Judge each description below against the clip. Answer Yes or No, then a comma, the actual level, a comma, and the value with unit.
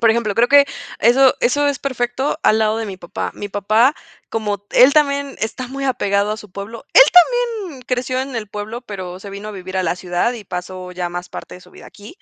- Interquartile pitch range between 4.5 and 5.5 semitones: Yes, average, 4.9 semitones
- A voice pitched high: Yes, high, 225 Hz